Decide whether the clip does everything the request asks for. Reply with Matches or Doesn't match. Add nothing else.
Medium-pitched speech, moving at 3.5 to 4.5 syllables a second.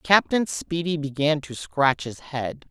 Matches